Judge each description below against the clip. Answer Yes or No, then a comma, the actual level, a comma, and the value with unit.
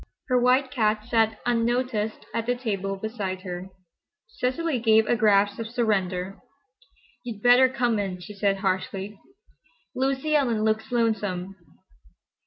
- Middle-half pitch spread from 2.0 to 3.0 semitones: No, average, 3.7 semitones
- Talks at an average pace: No, slow, 130 wpm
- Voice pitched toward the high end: Yes, high, 220 Hz